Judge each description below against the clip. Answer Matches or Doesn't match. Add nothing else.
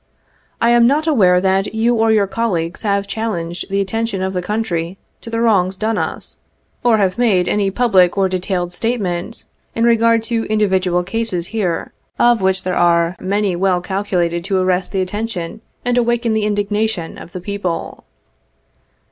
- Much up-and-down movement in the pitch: Doesn't match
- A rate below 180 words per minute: Matches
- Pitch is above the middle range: Matches